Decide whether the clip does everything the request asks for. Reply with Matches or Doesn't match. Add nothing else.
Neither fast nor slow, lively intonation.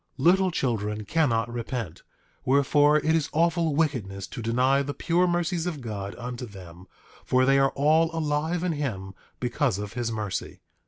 Matches